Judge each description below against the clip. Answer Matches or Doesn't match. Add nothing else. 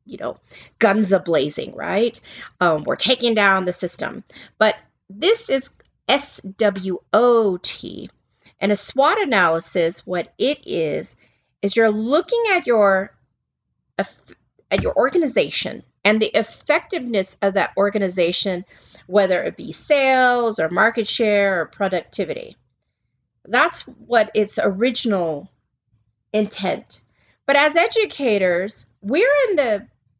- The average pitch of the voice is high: Matches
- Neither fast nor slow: Doesn't match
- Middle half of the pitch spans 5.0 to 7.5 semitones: Matches